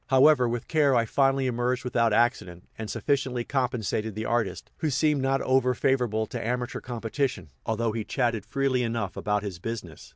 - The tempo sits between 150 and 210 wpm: Yes, average, 170 wpm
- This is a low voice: Yes, low, 120 Hz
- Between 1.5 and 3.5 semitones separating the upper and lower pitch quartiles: Yes, average, 3.1 semitones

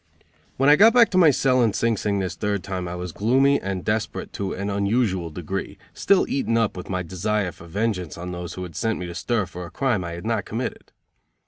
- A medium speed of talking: No, fast, 235 wpm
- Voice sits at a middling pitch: No, low, 100 Hz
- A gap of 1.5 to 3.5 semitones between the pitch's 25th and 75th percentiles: No, average, 4.4 semitones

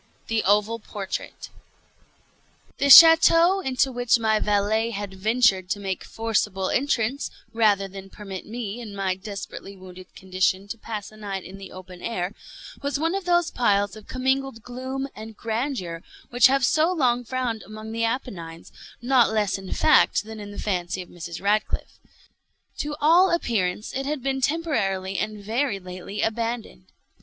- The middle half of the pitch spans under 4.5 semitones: No, average, 4.8 semitones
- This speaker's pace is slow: No, average, 160 wpm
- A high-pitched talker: Yes, high, 220 Hz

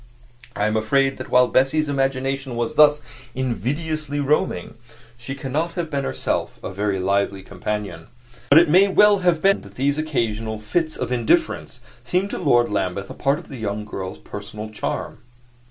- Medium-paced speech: Yes, average, 170 wpm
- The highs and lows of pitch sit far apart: Yes, wide, 6.1 semitones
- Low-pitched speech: Yes, low, 130 Hz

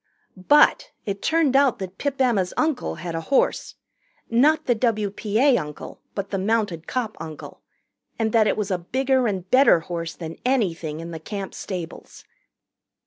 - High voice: Yes, high, 210 Hz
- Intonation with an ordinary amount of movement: No, wide, 6.7 semitones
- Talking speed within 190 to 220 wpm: No, average, 160 wpm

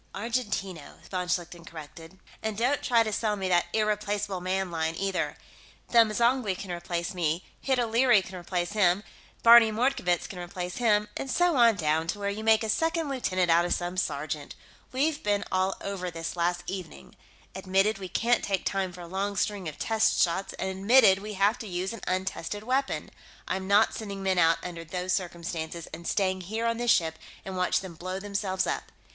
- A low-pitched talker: No, high, 190 Hz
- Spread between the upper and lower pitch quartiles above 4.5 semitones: No, average, 3.6 semitones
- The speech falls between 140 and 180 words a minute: No, average, 190 wpm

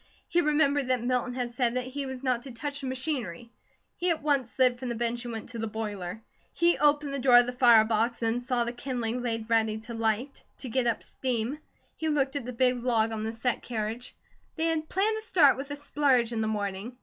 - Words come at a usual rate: No, fast, 235 wpm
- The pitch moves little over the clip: No, average, 3.3 semitones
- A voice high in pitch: Yes, high, 245 Hz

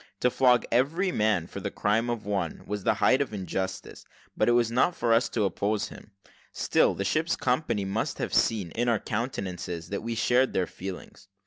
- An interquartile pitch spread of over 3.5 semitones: Yes, average, 4.0 semitones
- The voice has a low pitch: Yes, low, 110 Hz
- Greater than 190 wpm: Yes, average, 200 wpm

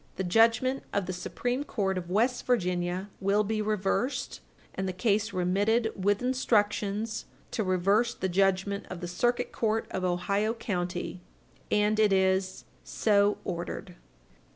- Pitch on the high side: Yes, high, 200 Hz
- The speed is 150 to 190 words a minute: No, average, 140 wpm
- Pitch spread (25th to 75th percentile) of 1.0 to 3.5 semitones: Yes, average, 3.1 semitones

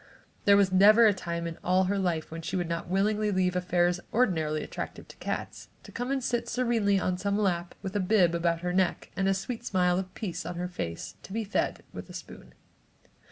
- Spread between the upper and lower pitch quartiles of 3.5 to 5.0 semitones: No, narrow, 2.6 semitones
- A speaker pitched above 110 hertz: Yes, medium, 185 Hz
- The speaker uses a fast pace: Yes, fast, 215 wpm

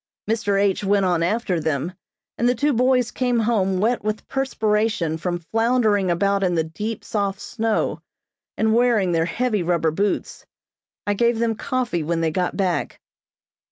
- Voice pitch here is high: Yes, high, 205 Hz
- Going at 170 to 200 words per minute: No, average, 160 wpm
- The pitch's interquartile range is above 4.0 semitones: Yes, average, 4.5 semitones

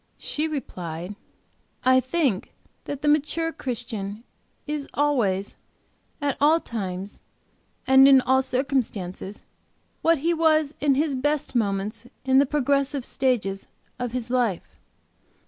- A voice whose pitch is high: Yes, very high, 260 Hz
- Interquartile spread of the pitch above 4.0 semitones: Yes, wide, 5.5 semitones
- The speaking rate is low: Yes, slow, 120 wpm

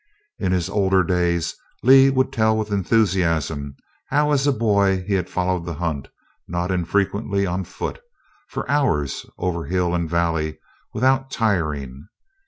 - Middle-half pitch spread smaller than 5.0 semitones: Yes, average, 4.4 semitones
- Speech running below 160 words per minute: Yes, average, 145 wpm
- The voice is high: No, very low, 95 Hz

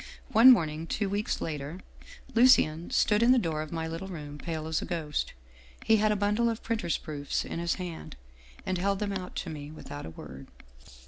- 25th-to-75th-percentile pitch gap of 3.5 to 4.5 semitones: No, average, 5.1 semitones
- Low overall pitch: No, medium, 170 Hz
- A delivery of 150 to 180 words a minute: No, fast, 205 wpm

